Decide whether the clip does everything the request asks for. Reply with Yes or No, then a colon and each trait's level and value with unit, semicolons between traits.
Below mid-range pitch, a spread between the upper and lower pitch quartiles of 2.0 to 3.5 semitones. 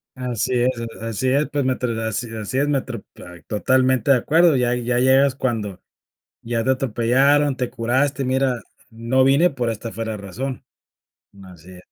Yes: low, 125 Hz; average, 2.8 semitones